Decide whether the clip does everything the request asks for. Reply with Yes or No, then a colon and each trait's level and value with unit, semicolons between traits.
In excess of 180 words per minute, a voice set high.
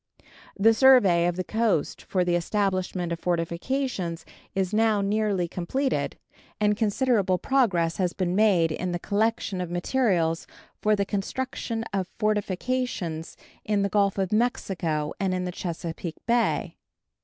No: average, 140 wpm; high, 195 Hz